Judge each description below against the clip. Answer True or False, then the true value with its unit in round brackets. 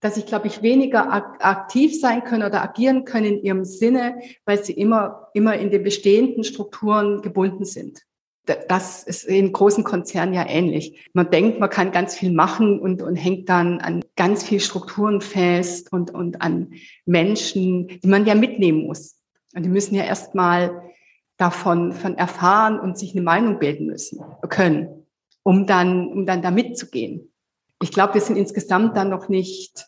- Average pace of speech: True (170 wpm)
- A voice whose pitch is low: False (195 Hz)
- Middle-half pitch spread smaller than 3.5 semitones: True (2.9 semitones)